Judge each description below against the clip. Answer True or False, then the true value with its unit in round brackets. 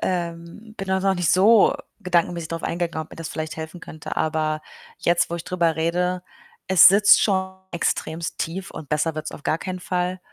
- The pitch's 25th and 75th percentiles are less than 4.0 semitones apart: True (2.4 semitones)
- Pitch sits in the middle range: True (170 Hz)